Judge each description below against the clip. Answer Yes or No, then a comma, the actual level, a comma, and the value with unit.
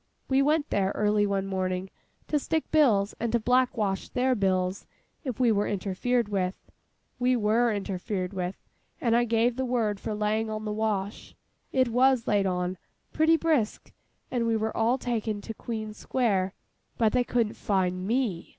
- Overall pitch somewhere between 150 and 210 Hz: No, high, 220 Hz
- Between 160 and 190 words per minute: Yes, average, 165 wpm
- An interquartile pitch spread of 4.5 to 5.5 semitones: No, average, 3.8 semitones